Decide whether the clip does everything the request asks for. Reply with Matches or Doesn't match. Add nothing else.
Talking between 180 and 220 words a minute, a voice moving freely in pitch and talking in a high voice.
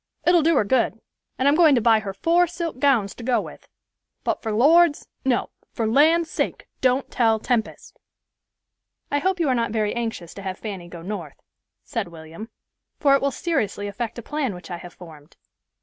Matches